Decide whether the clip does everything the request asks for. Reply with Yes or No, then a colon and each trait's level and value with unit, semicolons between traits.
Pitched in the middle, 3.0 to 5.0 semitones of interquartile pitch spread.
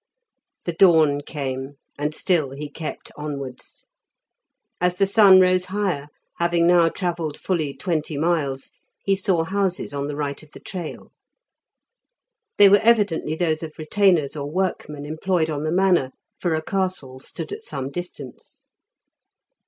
Yes: medium, 165 Hz; average, 4.1 semitones